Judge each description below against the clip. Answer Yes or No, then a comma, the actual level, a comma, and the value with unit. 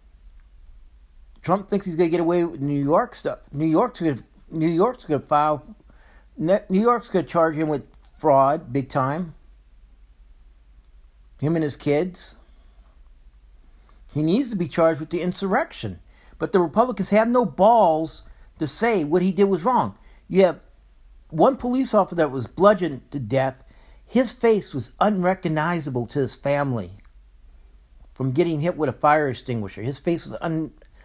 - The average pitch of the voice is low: No, medium, 150 Hz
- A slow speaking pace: No, average, 155 wpm